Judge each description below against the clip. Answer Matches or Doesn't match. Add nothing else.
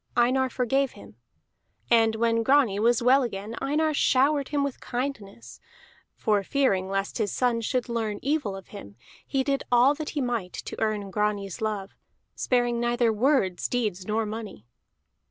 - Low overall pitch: Doesn't match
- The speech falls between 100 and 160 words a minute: Matches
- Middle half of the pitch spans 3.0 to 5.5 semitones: Matches